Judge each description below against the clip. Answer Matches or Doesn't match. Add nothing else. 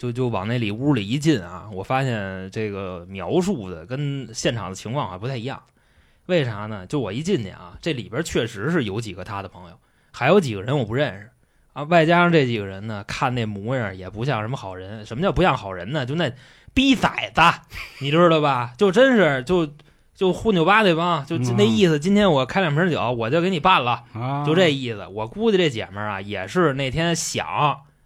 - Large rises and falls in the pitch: Matches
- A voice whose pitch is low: Matches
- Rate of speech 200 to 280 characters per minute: Doesn't match